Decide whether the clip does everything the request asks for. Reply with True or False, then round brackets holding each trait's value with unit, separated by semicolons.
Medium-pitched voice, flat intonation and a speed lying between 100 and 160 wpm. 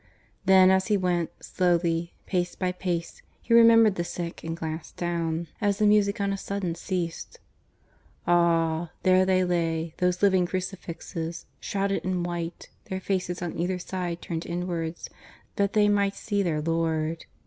True (180 Hz; 2.2 semitones; 155 wpm)